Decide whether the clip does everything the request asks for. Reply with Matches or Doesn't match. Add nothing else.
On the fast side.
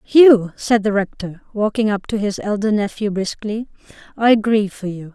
Doesn't match